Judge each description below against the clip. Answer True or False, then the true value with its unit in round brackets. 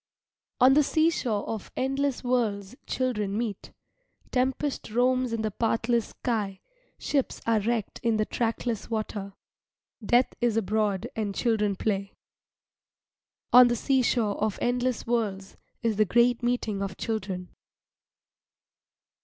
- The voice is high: True (230 Hz)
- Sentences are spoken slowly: True (120 wpm)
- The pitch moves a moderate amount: True (3.0 semitones)